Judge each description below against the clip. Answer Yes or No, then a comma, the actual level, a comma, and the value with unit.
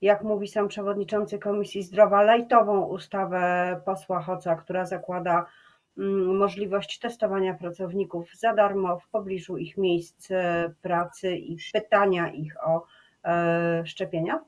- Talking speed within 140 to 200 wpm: No, slow, 110 wpm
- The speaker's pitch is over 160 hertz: Yes, high, 190 Hz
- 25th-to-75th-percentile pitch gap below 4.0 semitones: Yes, average, 2.8 semitones